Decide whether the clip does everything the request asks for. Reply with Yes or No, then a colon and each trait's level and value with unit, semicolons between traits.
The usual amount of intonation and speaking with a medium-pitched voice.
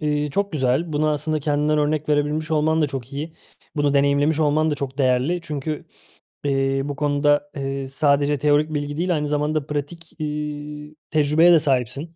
No: narrow, 1.5 semitones; medium, 150 Hz